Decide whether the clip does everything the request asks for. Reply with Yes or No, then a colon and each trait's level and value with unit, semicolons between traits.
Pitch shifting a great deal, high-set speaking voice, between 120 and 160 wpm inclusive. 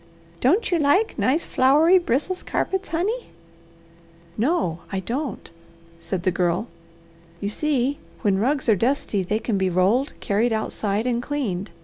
Yes: wide, 6.9 semitones; high, 245 Hz; average, 140 wpm